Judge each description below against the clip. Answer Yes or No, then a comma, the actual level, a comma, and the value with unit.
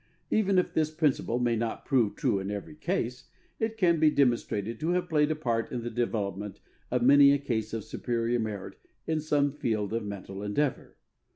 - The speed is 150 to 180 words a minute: No, average, 190 wpm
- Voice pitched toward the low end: Yes, low, 120 Hz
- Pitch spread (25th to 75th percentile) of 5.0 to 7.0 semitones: Yes, wide, 5.6 semitones